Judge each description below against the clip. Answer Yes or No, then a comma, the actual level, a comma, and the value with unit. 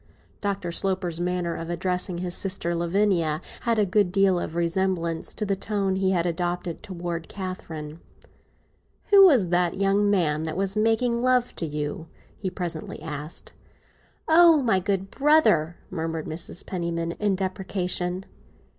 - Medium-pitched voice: Yes, medium, 180 Hz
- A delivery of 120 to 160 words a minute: Yes, average, 145 wpm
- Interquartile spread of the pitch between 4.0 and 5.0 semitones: No, average, 2.8 semitones